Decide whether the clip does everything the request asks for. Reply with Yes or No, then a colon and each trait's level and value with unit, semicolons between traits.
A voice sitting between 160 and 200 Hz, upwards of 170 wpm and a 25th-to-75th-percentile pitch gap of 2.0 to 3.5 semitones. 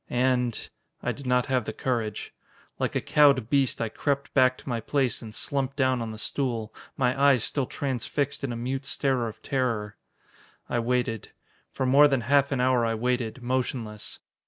No: low, 125 Hz; average, 180 wpm; narrow, 2.6 semitones